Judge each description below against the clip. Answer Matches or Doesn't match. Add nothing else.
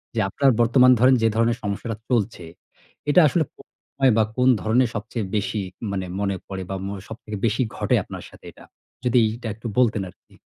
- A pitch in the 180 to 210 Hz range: Doesn't match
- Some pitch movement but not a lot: Matches